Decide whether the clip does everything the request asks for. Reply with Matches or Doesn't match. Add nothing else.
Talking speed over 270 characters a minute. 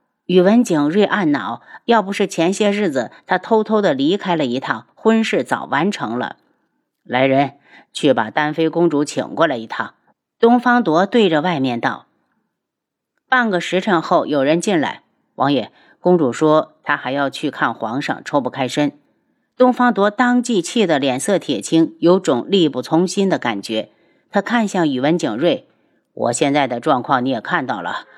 Doesn't match